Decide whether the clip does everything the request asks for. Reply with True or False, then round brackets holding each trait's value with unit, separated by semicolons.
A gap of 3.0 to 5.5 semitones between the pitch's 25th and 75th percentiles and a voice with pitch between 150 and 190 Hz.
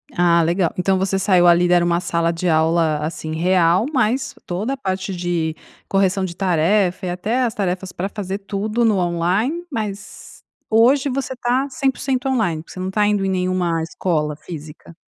True (3.8 semitones; 185 Hz)